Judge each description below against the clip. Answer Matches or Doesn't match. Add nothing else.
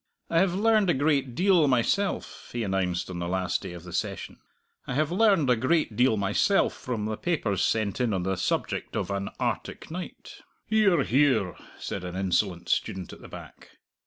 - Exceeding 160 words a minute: Matches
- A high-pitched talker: Doesn't match